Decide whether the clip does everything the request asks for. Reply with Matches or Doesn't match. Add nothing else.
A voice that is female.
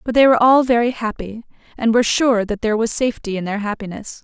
Matches